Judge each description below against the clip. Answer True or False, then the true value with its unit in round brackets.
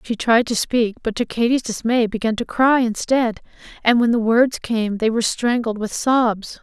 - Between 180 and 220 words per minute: True (200 wpm)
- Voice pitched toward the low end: False (230 Hz)